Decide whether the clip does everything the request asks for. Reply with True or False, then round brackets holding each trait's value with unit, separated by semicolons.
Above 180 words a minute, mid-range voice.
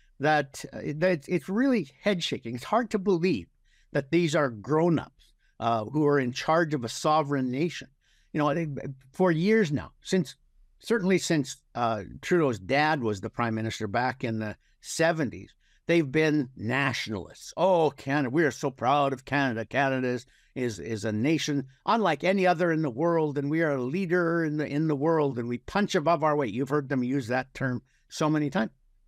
True (190 wpm; 145 Hz)